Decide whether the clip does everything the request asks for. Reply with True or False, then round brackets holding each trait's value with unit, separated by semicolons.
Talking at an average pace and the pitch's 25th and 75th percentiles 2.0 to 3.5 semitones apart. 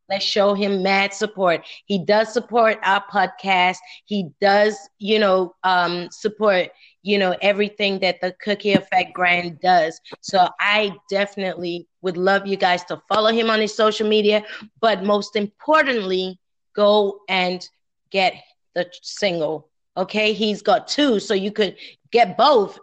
True (145 wpm; 2.6 semitones)